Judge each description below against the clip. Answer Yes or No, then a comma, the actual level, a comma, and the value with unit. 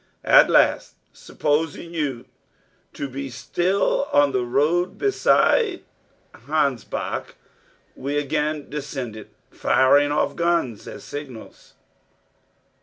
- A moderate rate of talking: No, slow, 100 wpm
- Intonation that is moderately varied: Yes, average, 3.5 semitones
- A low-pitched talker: No, medium, 145 Hz